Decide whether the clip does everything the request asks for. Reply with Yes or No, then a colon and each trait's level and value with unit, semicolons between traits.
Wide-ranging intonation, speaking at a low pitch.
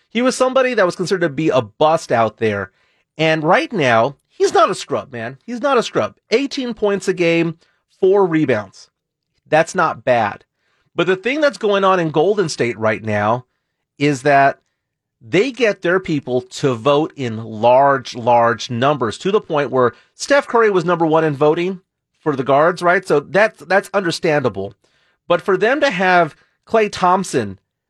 No: wide, 6.6 semitones; medium, 165 Hz